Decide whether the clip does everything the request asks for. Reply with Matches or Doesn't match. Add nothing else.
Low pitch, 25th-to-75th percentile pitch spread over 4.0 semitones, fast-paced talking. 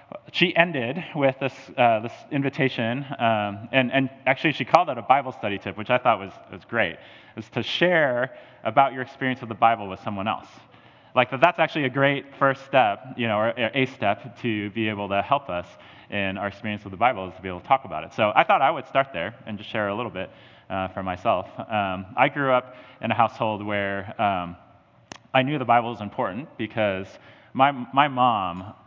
Matches